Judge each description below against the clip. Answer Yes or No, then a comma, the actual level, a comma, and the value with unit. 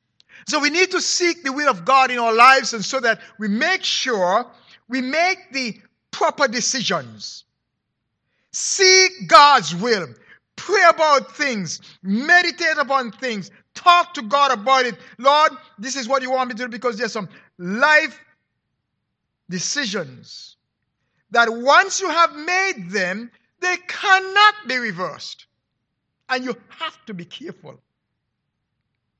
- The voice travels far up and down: Yes, wide, 6.0 semitones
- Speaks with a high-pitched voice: Yes, very high, 265 Hz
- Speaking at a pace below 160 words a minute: Yes, average, 140 wpm